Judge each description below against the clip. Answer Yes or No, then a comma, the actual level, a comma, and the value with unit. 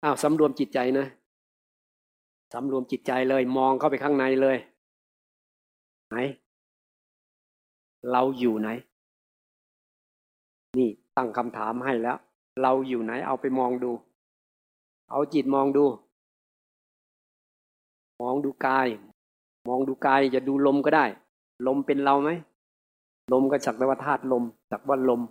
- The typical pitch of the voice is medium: No, low, 130 Hz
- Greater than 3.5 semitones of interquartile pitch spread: No, narrow, 2.4 semitones